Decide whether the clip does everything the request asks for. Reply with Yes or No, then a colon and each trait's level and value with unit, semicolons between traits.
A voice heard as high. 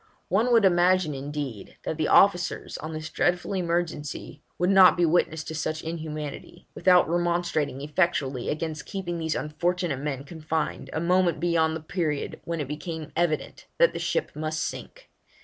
No: medium, 160 Hz